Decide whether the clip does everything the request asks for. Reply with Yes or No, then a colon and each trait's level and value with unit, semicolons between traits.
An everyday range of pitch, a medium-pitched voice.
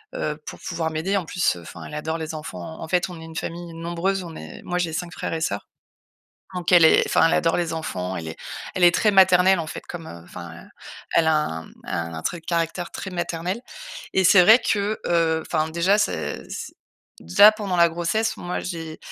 No: narrow, 2.1 semitones; medium, 165 Hz